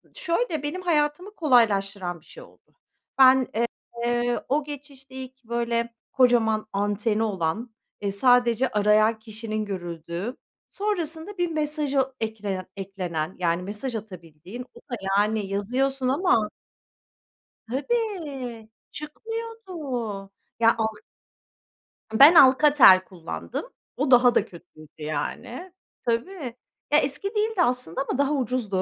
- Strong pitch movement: Yes, wide, 6.1 semitones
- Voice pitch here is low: No, high, 240 Hz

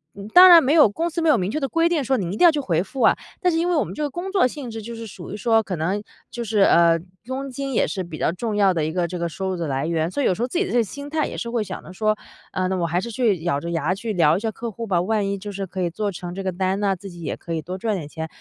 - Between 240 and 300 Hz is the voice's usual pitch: No, high, 200 Hz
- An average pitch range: No, wide, 6.2 semitones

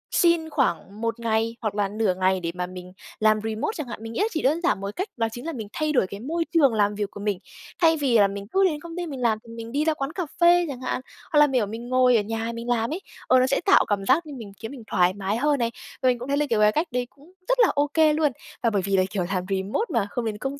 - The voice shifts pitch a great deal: Yes, wide, 6.1 semitones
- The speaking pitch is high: Yes, high, 235 Hz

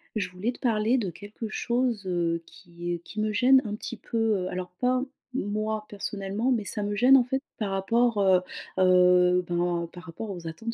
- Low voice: No, high, 205 Hz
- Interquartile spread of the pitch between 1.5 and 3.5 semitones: No, average, 4.1 semitones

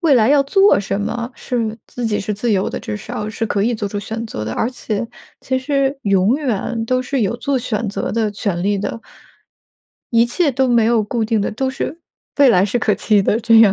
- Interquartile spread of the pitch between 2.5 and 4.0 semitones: Yes, average, 3.5 semitones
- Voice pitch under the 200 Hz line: No, high, 225 Hz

